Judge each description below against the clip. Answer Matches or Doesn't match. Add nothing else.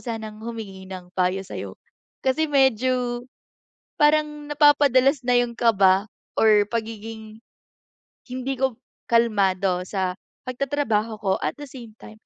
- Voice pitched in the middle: Doesn't match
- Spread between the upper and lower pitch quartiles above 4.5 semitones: Doesn't match